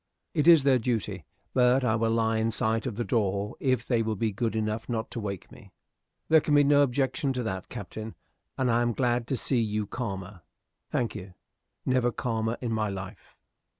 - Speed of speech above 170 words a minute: Yes, average, 200 wpm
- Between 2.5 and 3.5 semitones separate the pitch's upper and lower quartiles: Yes, average, 2.8 semitones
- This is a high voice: No, low, 115 Hz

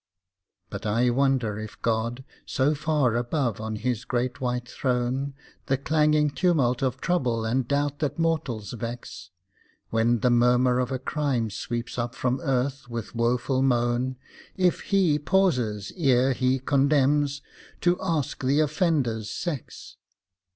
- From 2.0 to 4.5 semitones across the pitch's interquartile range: Yes, average, 3.2 semitones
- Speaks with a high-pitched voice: No, low, 130 Hz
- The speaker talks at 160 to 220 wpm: No, slow, 135 wpm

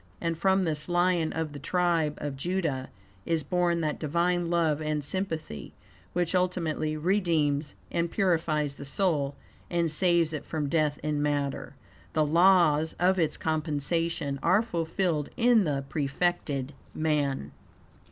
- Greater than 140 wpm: No, slow, 135 wpm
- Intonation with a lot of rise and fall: No, average, 3.0 semitones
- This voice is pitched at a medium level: Yes, medium, 160 Hz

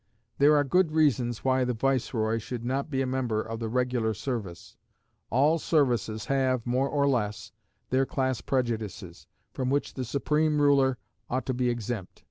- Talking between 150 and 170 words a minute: Yes, average, 165 wpm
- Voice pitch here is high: No, low, 130 Hz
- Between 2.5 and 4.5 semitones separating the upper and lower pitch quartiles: Yes, average, 2.9 semitones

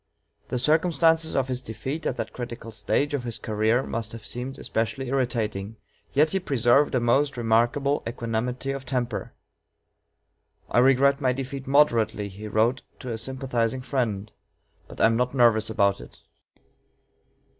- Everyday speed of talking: Yes, average, 150 wpm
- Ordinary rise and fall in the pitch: Yes, average, 3.3 semitones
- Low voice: Yes, low, 125 Hz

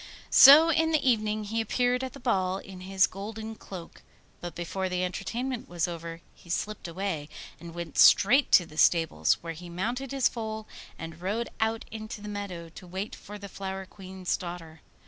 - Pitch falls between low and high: No, high, 195 Hz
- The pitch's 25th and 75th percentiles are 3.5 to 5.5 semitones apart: Yes, average, 4.2 semitones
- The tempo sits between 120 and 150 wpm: No, average, 185 wpm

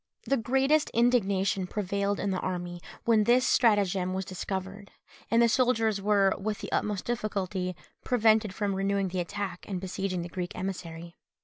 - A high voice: Yes, high, 200 Hz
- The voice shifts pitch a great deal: No, average, 2.9 semitones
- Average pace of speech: Yes, average, 155 wpm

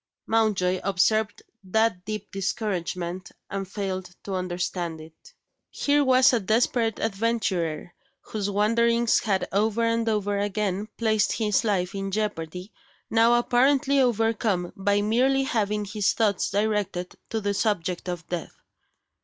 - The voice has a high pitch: Yes, high, 205 Hz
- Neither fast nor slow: No, slow, 130 wpm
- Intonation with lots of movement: No, average, 3.3 semitones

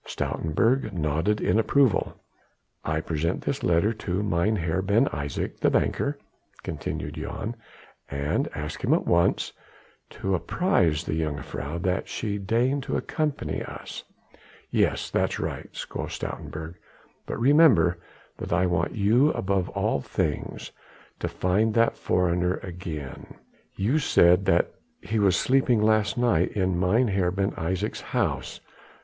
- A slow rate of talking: Yes, slow, 130 wpm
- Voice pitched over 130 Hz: No, very low, 95 Hz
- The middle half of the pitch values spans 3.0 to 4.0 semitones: No, average, 4.8 semitones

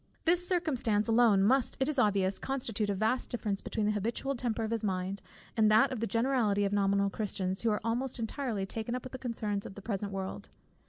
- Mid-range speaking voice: No, high, 220 Hz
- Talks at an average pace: No, fast, 215 wpm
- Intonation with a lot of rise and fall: No, average, 3.6 semitones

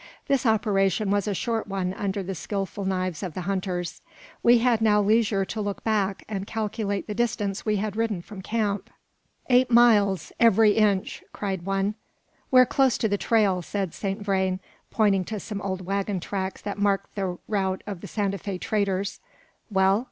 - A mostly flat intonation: Yes, narrow, 2.1 semitones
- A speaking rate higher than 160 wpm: Yes, average, 175 wpm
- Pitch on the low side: No, high, 200 Hz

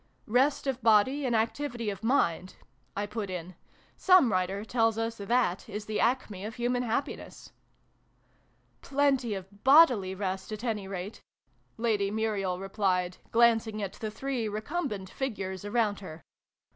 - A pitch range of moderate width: Yes, average, 3.7 semitones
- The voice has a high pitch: Yes, high, 215 Hz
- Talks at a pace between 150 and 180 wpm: Yes, average, 160 wpm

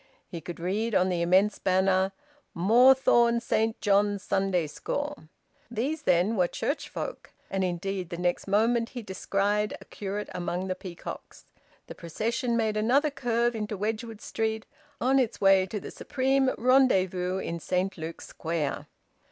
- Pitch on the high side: Yes, high, 205 Hz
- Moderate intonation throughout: Yes, average, 4.2 semitones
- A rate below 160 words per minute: Yes, average, 150 wpm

